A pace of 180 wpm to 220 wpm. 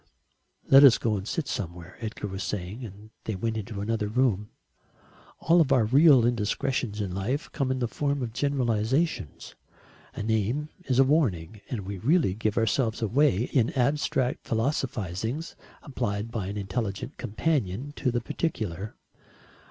No: average, 150 wpm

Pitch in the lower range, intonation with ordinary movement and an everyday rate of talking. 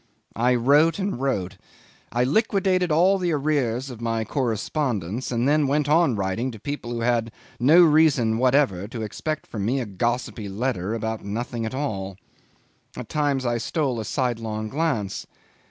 Yes: low, 125 Hz; average, 4.8 semitones; average, 160 wpm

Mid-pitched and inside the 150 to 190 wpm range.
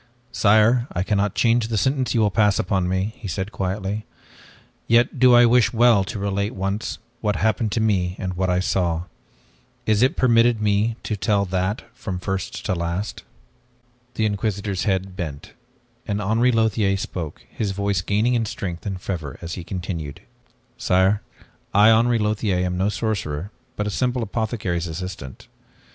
No: low, 100 Hz; average, 165 wpm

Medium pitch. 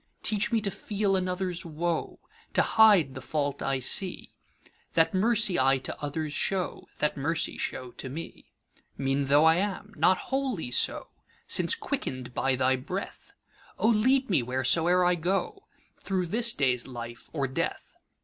Yes: medium, 170 Hz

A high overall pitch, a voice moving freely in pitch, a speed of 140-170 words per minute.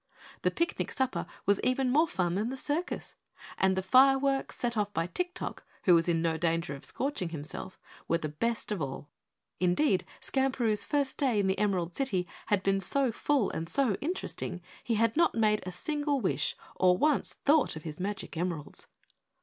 No: high, 210 Hz; wide, 7.3 semitones; average, 180 wpm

